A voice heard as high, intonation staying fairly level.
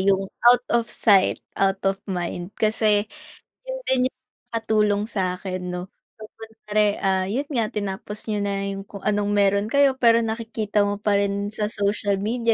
Yes: high, 205 Hz; narrow, 2.1 semitones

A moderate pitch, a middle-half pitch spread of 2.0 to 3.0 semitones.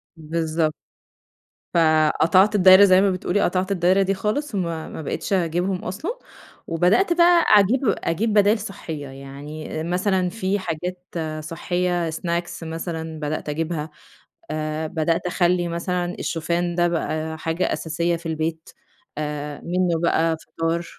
Yes: medium, 170 Hz; narrow, 2.6 semitones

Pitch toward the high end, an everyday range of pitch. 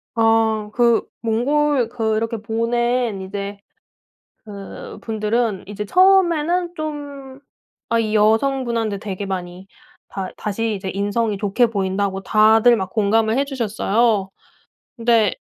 Yes: high, 225 Hz; average, 3.0 semitones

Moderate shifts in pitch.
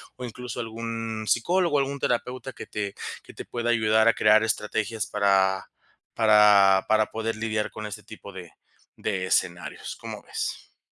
No: narrow, 2.2 semitones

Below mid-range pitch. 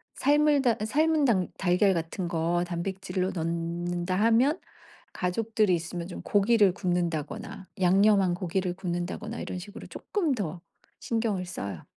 No: medium, 185 Hz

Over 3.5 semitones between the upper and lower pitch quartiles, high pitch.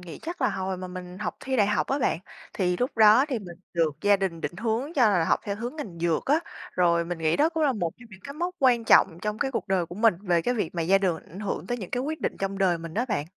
Yes: wide, 5.6 semitones; high, 200 Hz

